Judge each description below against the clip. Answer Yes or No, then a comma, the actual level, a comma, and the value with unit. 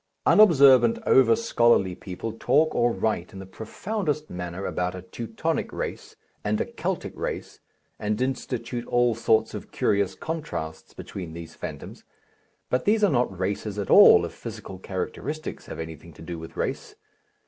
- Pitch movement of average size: No, wide, 6.3 semitones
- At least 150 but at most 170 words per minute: Yes, average, 155 wpm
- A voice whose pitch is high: No, low, 110 Hz